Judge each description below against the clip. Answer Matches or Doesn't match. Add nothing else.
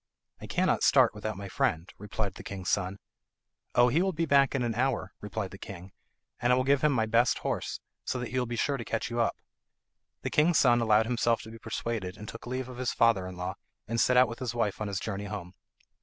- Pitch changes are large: Doesn't match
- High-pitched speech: Doesn't match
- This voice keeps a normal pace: Doesn't match